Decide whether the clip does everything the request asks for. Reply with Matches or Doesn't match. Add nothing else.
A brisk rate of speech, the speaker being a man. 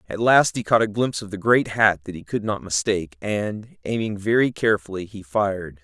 Matches